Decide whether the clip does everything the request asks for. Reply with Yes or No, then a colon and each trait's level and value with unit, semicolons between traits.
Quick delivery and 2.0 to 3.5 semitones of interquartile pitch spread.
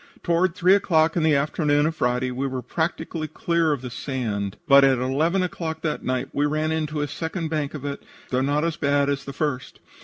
Yes: fast, 215 wpm; average, 3.0 semitones